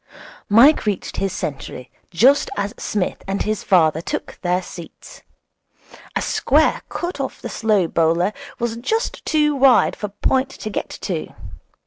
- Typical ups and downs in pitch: No, wide, 6.5 semitones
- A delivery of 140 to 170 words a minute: Yes, average, 145 wpm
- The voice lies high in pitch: Yes, high, 205 Hz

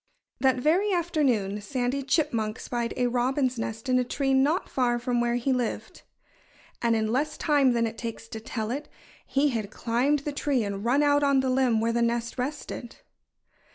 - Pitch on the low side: No, very high, 250 Hz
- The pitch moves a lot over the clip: No, average, 3.1 semitones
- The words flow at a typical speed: Yes, average, 190 wpm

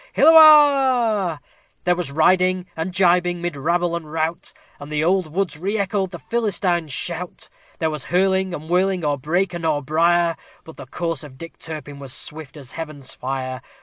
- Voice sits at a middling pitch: Yes, medium, 170 Hz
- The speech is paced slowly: No, average, 175 wpm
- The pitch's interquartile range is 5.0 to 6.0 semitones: No, average, 3.4 semitones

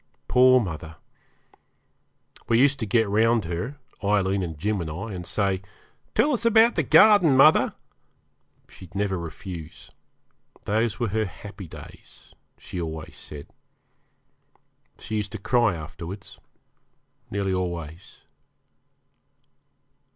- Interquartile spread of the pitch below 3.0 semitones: No, average, 5.3 semitones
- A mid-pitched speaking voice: No, low, 100 Hz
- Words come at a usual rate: No, slow, 115 wpm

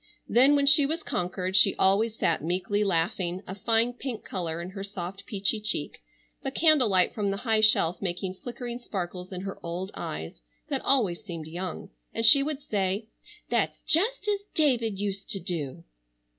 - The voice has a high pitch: Yes, high, 200 Hz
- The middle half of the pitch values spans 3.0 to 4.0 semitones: No, average, 4.7 semitones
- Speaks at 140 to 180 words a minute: Yes, average, 175 wpm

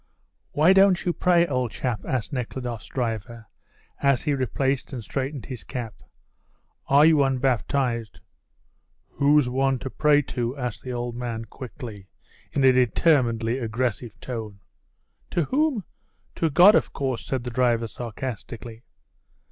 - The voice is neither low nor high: No, low, 125 Hz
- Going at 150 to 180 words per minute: No, slow, 135 wpm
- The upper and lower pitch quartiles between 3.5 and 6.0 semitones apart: No, average, 3.1 semitones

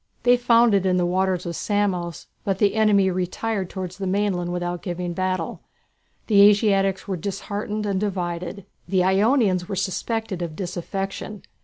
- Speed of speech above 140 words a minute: Yes, average, 155 wpm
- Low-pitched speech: No, high, 190 Hz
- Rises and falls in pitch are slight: Yes, narrow, 2.3 semitones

